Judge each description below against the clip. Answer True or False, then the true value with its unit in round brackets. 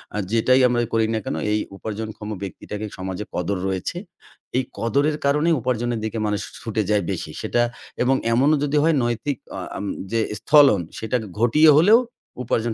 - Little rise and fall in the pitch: False (4.6 semitones)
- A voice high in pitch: False (115 Hz)